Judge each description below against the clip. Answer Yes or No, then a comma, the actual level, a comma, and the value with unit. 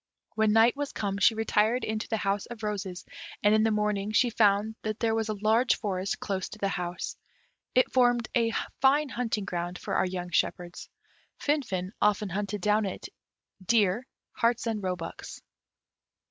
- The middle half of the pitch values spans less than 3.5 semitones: Yes, average, 2.8 semitones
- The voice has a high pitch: Yes, high, 210 Hz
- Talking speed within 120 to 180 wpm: Yes, average, 175 wpm